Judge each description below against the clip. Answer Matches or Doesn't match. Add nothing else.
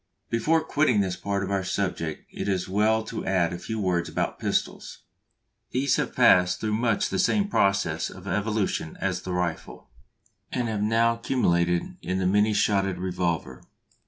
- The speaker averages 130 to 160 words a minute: Doesn't match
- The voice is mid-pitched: Doesn't match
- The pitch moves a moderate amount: Matches